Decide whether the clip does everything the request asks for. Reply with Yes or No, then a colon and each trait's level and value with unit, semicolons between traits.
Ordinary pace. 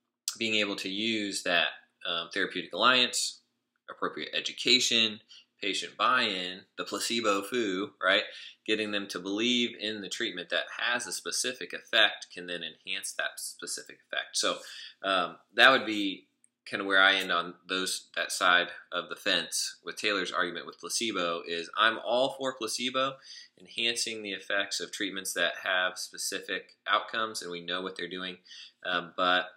Yes: average, 160 wpm